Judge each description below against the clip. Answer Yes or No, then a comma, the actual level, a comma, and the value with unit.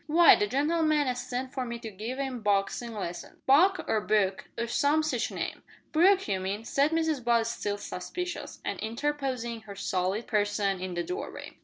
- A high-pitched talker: Yes, high, 235 Hz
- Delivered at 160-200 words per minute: Yes, average, 180 wpm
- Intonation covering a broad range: Yes, wide, 6.2 semitones